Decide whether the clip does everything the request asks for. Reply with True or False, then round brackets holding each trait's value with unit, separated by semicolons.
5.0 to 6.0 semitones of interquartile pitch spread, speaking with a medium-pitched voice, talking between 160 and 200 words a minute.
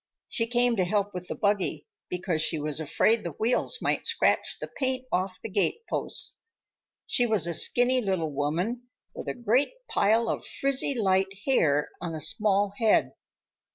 False (5.5 semitones; 205 Hz; 165 wpm)